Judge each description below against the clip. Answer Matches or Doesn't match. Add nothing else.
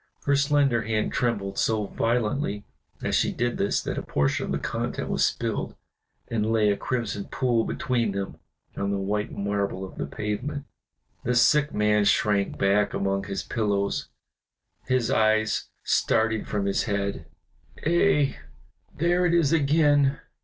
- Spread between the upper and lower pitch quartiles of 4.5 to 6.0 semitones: Matches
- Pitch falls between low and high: Doesn't match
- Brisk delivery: Doesn't match